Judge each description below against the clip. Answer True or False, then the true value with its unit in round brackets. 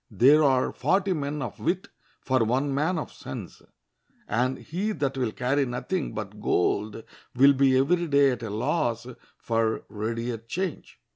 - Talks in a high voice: False (130 Hz)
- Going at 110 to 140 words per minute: False (155 wpm)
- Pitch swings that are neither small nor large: True (4.4 semitones)